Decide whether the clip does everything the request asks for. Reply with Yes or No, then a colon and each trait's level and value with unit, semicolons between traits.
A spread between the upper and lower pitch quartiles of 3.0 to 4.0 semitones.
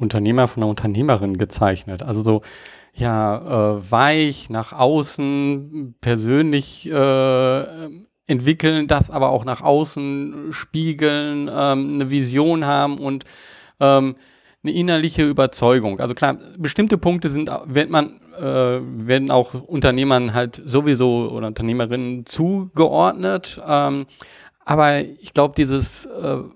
Yes: average, 3.5 semitones